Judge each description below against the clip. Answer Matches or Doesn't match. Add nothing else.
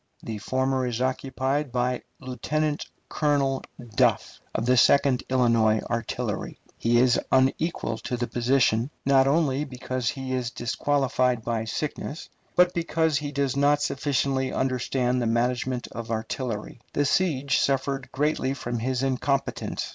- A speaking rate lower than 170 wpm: Matches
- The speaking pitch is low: Matches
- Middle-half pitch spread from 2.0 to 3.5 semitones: Matches